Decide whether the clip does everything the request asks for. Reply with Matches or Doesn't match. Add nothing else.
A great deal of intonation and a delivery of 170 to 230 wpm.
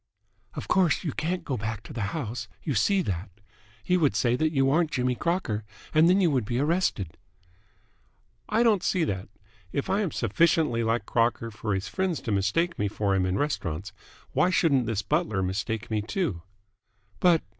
Matches